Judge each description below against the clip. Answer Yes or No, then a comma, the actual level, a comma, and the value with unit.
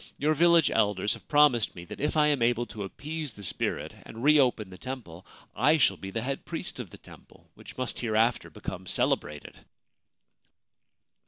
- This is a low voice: Yes, low, 120 Hz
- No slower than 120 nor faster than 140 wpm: No, average, 175 wpm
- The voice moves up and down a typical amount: No, wide, 6.1 semitones